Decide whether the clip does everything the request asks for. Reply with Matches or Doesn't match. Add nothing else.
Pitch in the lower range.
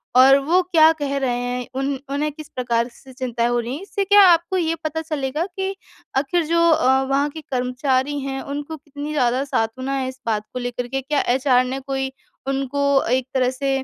Doesn't match